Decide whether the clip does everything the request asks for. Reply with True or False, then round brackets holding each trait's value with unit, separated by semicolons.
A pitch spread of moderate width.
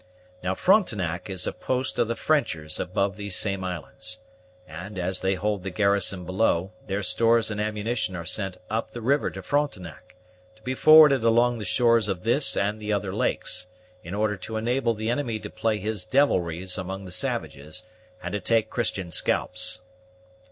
True (3.7 semitones)